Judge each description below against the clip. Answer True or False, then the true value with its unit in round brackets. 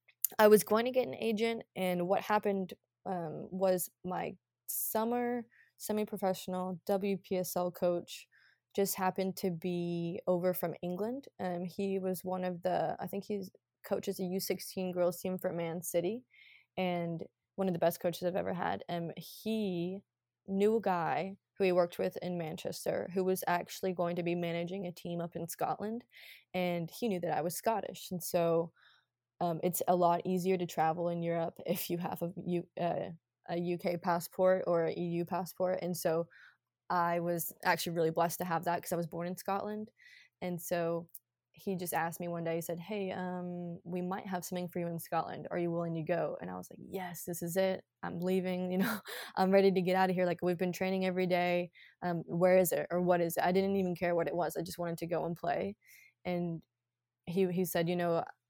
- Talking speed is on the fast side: True (210 wpm)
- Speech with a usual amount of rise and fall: False (1.6 semitones)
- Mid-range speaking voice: True (180 Hz)